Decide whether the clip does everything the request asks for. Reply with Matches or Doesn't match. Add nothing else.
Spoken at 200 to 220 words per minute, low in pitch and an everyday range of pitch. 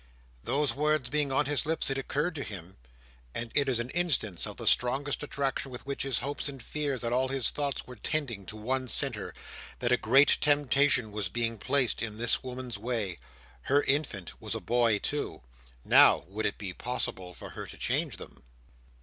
Doesn't match